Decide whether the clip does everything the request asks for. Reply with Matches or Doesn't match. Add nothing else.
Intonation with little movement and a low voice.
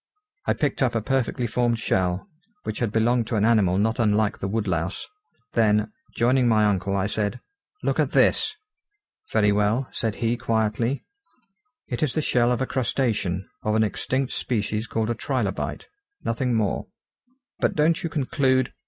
Doesn't match